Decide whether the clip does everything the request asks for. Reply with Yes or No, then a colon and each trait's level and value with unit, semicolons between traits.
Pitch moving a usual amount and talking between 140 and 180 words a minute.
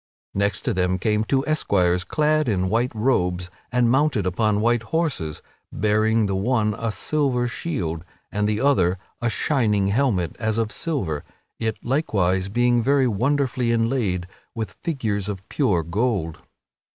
Yes: average, 5.0 semitones; average, 145 wpm